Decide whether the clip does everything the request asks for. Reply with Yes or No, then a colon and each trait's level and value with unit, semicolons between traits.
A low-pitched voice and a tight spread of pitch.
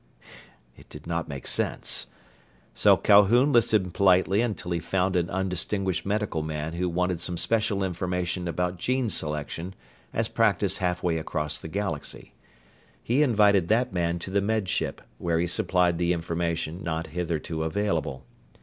No: very low, 90 Hz; average, 3.1 semitones